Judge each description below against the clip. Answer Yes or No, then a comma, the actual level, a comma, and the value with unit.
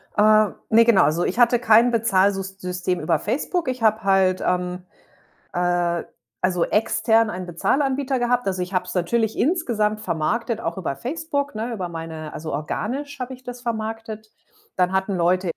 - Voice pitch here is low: No, high, 215 Hz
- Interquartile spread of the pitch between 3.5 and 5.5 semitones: Yes, average, 4.7 semitones